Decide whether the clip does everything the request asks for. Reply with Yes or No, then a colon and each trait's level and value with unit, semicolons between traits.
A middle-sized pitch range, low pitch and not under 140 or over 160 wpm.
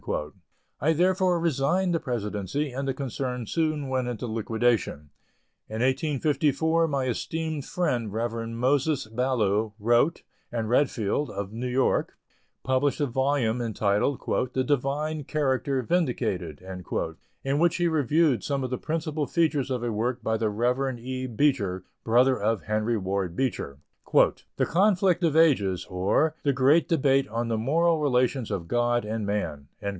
Yes: average, 4.7 semitones; low, 130 Hz; average, 145 wpm